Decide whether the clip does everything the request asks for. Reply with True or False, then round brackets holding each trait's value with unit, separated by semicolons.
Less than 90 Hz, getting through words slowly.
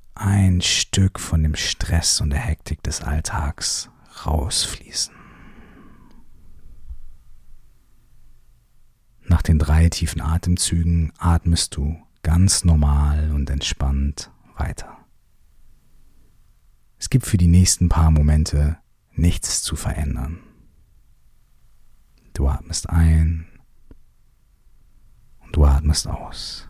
True (80 Hz; 90 wpm)